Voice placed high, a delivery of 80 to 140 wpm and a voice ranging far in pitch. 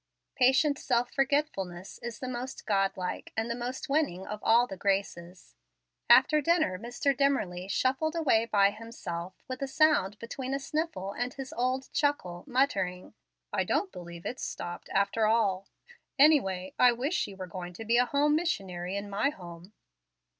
No: high, 230 Hz; average, 165 wpm; wide, 6.2 semitones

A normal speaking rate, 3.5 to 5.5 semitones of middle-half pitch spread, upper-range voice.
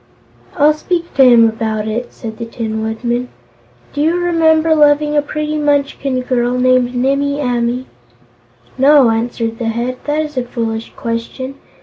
Yes: average, 150 wpm; average, 4.0 semitones; very high, 255 Hz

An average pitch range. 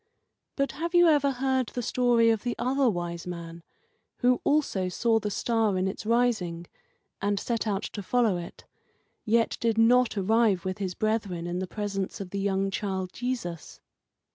Yes: average, 4.5 semitones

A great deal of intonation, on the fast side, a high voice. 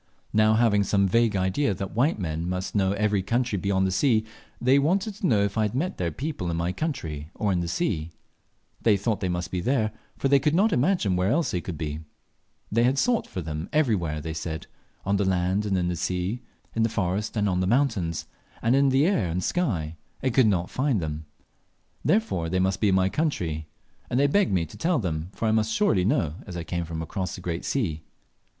No: wide, 5.8 semitones; fast, 230 wpm; low, 100 Hz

